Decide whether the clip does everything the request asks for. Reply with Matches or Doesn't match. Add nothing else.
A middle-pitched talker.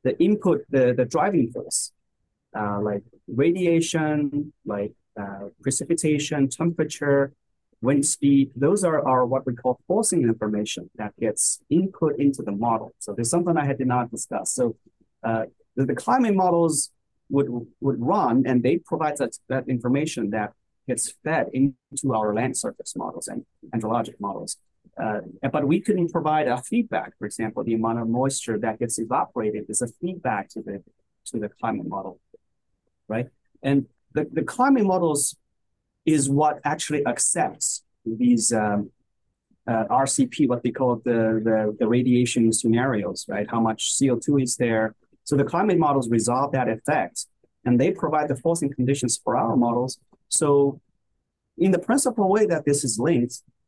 Doesn't match